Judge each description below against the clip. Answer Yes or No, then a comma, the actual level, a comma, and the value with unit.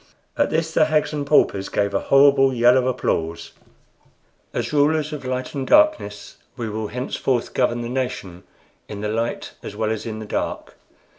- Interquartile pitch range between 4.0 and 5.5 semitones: Yes, average, 4.8 semitones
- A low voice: Yes, low, 125 Hz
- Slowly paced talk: No, average, 175 wpm